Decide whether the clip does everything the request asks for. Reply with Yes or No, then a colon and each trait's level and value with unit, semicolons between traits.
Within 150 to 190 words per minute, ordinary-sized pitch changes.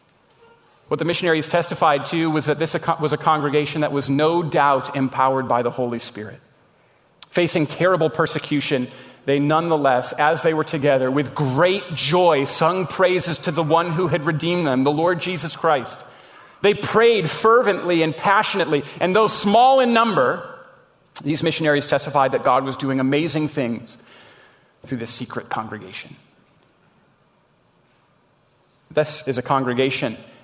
No: average, 140 wpm; average, 3.9 semitones